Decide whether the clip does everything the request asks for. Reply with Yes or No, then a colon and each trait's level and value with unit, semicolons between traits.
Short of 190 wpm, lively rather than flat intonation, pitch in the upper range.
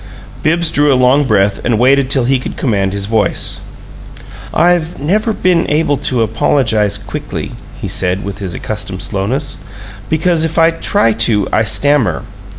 No: average, 155 wpm; wide, 6.9 semitones; low, 130 Hz